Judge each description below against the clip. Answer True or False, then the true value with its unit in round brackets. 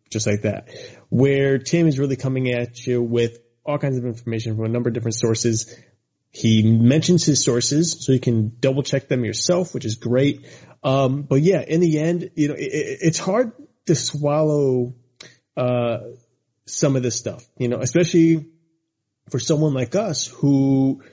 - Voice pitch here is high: False (135 Hz)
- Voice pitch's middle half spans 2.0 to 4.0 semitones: False (4.4 semitones)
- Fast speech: False (175 wpm)